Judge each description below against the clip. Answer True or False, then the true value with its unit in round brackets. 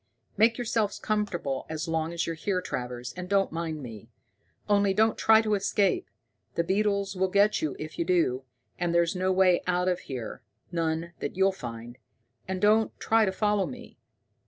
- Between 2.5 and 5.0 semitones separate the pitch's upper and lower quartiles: True (4.0 semitones)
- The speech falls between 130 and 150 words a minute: False (180 wpm)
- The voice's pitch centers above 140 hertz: True (185 Hz)